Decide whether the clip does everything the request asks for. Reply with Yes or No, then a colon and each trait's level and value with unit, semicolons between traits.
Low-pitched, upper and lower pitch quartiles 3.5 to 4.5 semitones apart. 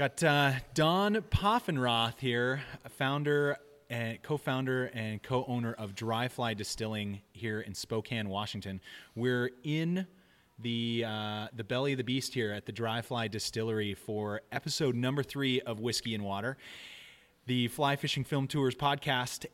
Yes: low, 125 Hz; average, 3.9 semitones